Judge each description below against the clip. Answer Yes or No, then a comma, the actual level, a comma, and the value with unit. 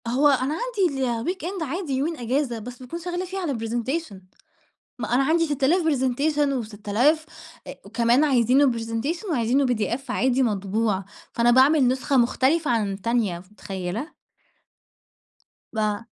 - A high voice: Yes, very high, 255 Hz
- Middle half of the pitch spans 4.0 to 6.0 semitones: Yes, average, 4.7 semitones